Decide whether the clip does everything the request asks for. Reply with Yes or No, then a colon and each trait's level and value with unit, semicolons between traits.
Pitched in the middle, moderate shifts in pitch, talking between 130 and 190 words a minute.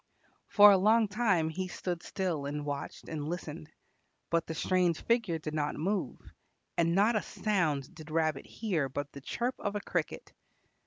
Yes: medium, 170 Hz; average, 4.9 semitones; average, 170 wpm